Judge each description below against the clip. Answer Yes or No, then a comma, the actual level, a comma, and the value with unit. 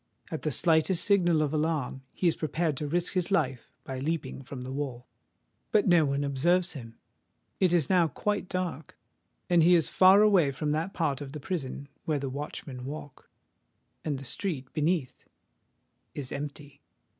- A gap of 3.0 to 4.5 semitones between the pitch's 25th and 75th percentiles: Yes, average, 4.1 semitones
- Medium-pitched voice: Yes, medium, 155 Hz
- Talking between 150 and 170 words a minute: Yes, average, 160 wpm